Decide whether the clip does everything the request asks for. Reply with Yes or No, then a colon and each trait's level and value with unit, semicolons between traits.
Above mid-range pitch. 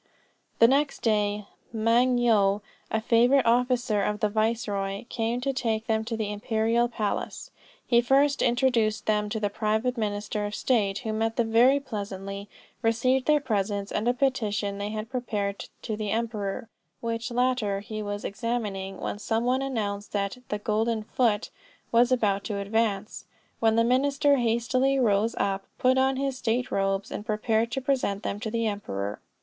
Yes: high, 225 Hz